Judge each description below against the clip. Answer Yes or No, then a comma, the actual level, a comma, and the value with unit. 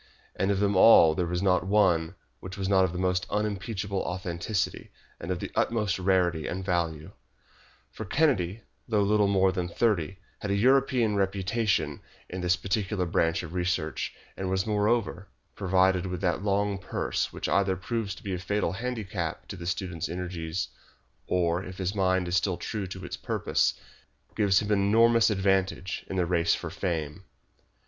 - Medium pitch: No, very low, 95 Hz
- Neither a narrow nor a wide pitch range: No, narrow, 2.3 semitones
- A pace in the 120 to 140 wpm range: No, average, 170 wpm